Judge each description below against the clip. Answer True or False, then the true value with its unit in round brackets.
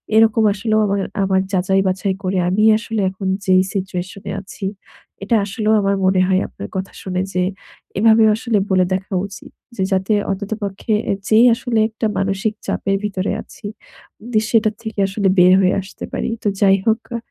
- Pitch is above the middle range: True (195 Hz)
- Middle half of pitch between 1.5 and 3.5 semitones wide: True (2.4 semitones)